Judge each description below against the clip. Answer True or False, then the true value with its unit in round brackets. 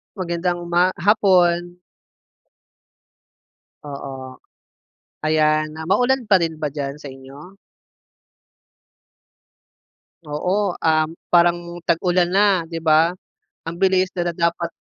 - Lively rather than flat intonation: False (2.8 semitones)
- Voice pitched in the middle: True (170 Hz)